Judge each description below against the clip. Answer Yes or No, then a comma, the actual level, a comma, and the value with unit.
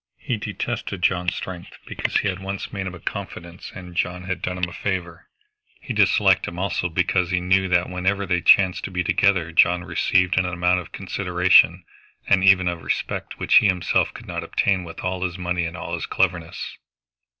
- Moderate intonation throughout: No, narrow, 1.4 semitones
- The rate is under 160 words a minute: No, average, 195 wpm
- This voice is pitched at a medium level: No, very low, 90 Hz